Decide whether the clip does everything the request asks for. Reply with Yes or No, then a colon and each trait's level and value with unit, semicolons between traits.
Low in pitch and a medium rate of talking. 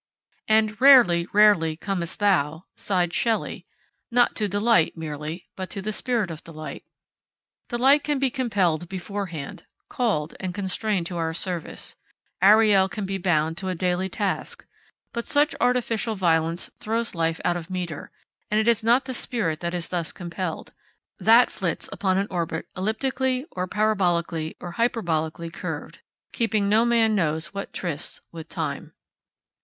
No: high, 190 Hz; average, 150 wpm